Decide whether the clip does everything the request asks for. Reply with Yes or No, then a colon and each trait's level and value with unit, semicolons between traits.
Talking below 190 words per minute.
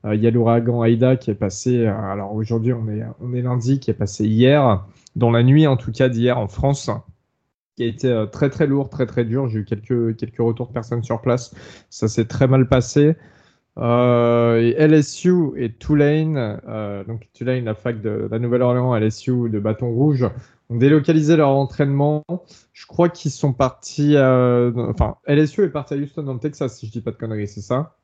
No: average, 210 wpm